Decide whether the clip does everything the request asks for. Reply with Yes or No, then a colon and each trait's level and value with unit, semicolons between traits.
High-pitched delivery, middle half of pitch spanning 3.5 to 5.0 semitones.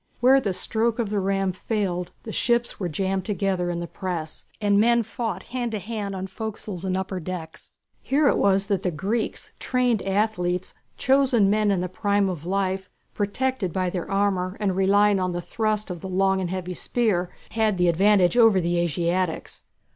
No: high, 195 Hz; average, 2.9 semitones